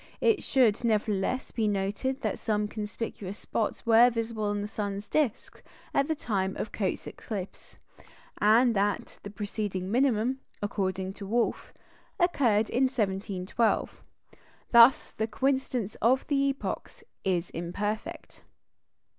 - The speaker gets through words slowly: Yes, slow, 120 wpm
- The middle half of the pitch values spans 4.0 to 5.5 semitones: No, average, 3.3 semitones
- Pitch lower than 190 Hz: No, high, 215 Hz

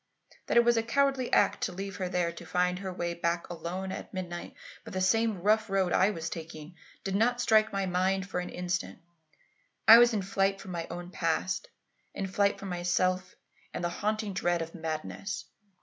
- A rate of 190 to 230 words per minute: Yes, average, 195 wpm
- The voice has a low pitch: No, medium, 185 Hz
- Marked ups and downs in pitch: No, narrow, 2.6 semitones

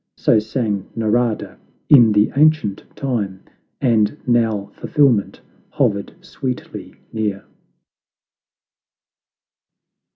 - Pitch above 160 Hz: No, low, 110 Hz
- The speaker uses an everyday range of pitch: Yes, average, 3.6 semitones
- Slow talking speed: Yes, slow, 75 wpm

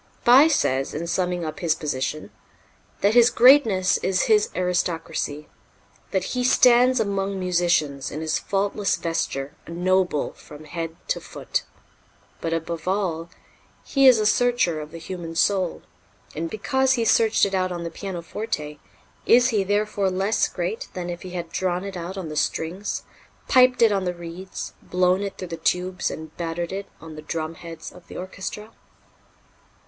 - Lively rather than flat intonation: No, average, 3.9 semitones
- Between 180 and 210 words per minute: No, average, 165 wpm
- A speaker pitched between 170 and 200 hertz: Yes, medium, 185 Hz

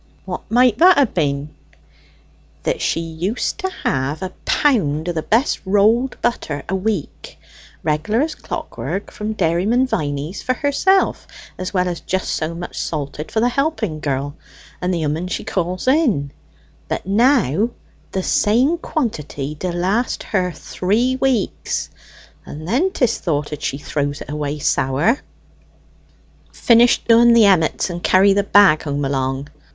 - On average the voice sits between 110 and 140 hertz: No, medium, 185 Hz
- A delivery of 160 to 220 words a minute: No, average, 145 wpm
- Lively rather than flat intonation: Yes, wide, 7.5 semitones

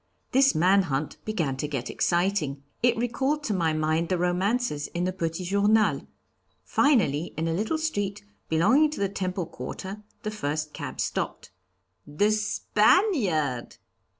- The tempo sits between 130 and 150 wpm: Yes, average, 145 wpm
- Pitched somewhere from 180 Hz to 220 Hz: Yes, high, 190 Hz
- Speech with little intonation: No, average, 5.3 semitones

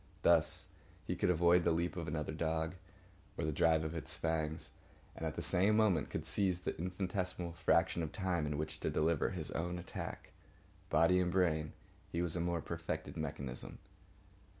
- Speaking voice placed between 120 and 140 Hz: No, very low, 85 Hz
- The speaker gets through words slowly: No, average, 175 wpm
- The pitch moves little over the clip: Yes, narrow, 2.2 semitones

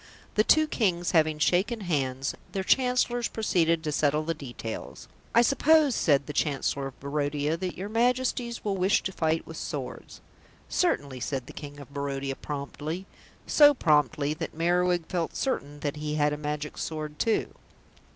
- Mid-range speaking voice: Yes, medium, 155 Hz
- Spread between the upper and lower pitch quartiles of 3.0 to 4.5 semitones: No, average, 5.3 semitones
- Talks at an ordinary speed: Yes, average, 160 wpm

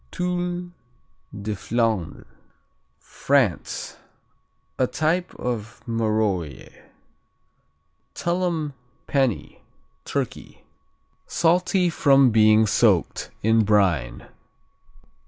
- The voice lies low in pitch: Yes, low, 115 Hz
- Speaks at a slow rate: Yes, slow, 65 wpm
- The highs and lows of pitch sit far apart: Yes, wide, 7.4 semitones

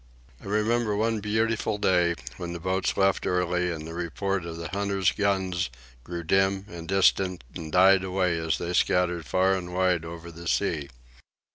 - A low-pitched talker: Yes, very low, 90 Hz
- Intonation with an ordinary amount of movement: No, narrow, 2.3 semitones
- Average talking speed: Yes, average, 170 wpm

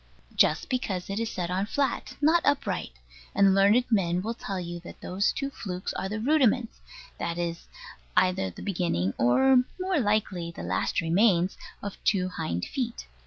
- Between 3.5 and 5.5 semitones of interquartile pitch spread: Yes, average, 5.2 semitones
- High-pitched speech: Yes, high, 195 Hz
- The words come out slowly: No, average, 165 wpm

